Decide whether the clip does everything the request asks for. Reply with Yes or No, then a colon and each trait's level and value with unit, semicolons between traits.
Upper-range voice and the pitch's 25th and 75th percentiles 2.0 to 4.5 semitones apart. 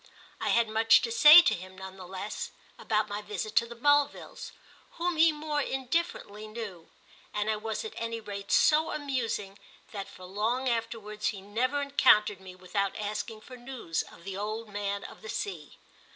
Yes: high, 215 Hz; average, 4.1 semitones